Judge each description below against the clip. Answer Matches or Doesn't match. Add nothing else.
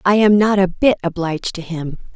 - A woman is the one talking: Matches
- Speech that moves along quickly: Matches